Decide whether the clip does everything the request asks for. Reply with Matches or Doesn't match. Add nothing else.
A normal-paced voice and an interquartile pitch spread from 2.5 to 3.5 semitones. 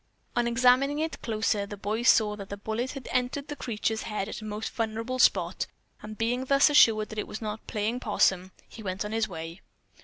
Doesn't match